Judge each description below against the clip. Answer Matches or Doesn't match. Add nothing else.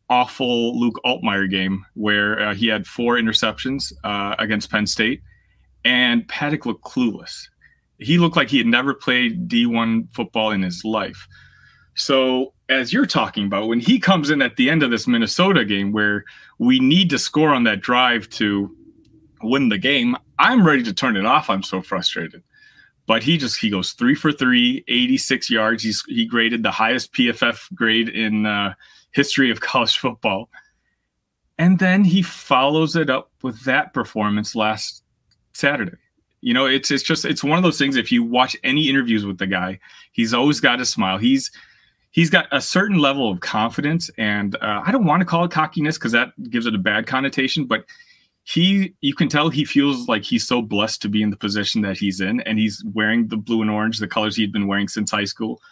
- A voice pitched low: Matches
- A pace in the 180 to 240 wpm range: Matches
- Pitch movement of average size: Doesn't match